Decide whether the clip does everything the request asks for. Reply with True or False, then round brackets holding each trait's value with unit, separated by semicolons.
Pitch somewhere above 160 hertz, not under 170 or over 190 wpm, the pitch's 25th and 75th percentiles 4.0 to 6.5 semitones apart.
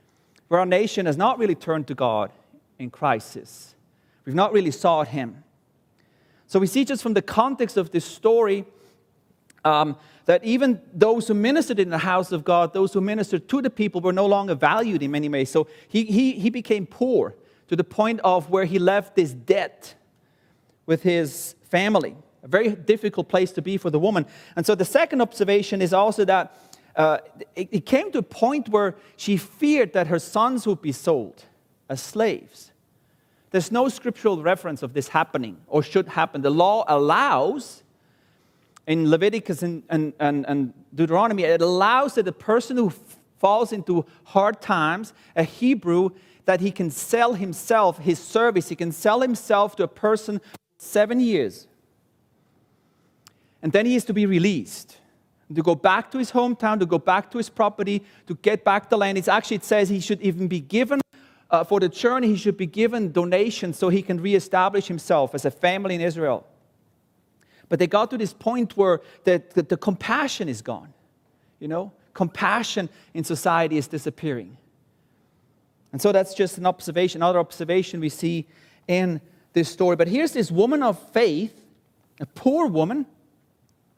True (185 Hz; 175 wpm; 4.3 semitones)